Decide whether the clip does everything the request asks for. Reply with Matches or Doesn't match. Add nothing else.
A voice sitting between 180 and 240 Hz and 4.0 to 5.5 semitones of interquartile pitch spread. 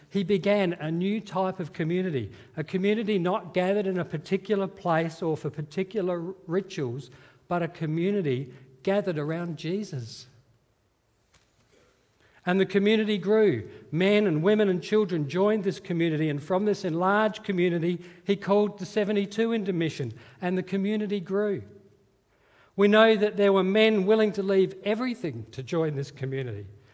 Matches